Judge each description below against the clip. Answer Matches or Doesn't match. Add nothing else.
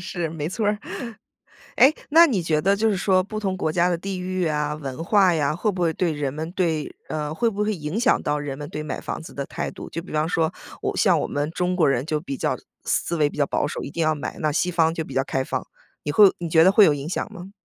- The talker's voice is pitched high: Doesn't match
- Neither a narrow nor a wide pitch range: Matches